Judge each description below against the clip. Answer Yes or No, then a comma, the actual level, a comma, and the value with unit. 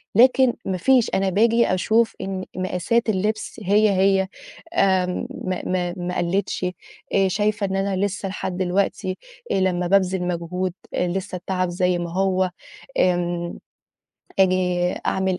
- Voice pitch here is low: No, medium, 185 Hz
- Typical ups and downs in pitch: No, narrow, 1.7 semitones